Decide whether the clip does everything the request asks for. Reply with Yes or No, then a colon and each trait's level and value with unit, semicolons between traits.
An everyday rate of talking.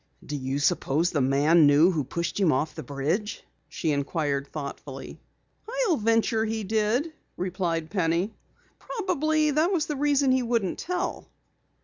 Yes: average, 145 wpm